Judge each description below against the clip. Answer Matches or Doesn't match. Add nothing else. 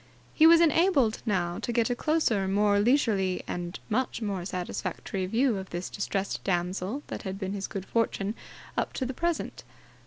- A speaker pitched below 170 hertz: Doesn't match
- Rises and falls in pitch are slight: Doesn't match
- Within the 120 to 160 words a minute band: Doesn't match